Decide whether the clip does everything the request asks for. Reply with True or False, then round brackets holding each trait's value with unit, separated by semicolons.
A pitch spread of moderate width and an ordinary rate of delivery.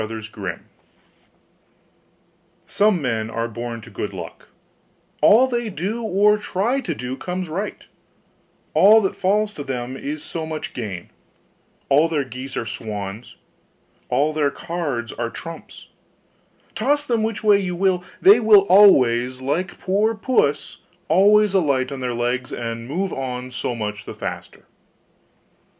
False (8.6 semitones; 145 wpm)